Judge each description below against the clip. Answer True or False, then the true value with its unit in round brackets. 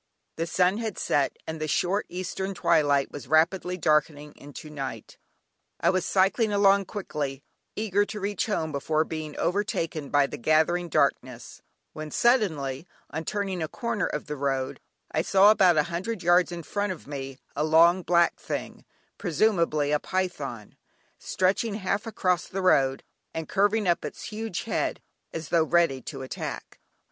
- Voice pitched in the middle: True (170 Hz)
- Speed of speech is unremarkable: True (160 wpm)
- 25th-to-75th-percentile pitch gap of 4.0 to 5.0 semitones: True (4.6 semitones)